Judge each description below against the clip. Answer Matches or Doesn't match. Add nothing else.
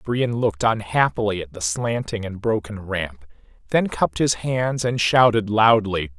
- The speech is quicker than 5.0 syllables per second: Doesn't match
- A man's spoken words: Matches